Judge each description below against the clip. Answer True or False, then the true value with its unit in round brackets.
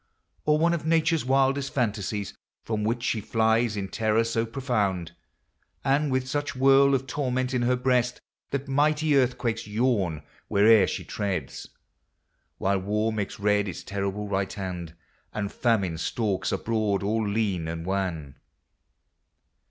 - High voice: False (110 Hz)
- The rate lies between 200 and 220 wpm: False (140 wpm)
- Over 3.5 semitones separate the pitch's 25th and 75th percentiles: True (4.7 semitones)